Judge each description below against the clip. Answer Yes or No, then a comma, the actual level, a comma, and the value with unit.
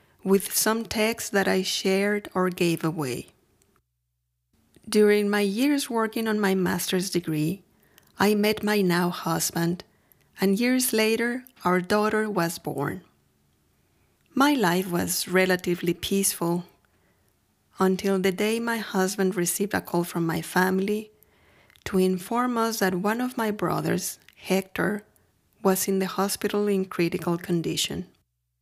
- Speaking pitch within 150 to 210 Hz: Yes, high, 190 Hz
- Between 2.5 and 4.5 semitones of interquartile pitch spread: Yes, average, 3.4 semitones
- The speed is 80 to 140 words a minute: Yes, average, 130 wpm